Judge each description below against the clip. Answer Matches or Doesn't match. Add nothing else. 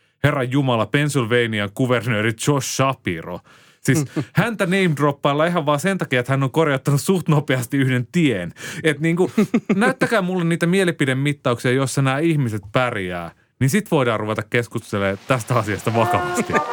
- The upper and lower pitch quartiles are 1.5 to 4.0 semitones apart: Doesn't match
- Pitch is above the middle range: Doesn't match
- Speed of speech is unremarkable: Matches